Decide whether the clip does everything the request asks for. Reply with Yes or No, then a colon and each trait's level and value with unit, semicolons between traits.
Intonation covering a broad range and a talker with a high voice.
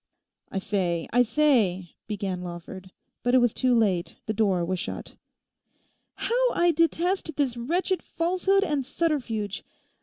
Yes: wide, 9.0 semitones; high, 240 Hz